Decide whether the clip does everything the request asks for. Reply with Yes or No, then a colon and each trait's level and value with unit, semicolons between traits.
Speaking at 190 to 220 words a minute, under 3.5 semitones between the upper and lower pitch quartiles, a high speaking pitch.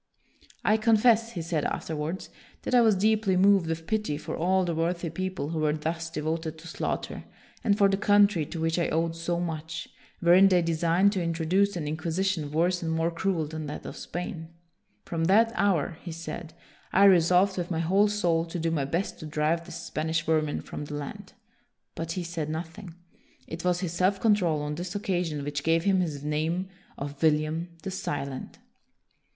No: average, 195 wpm; average, 2.9 semitones; medium, 170 Hz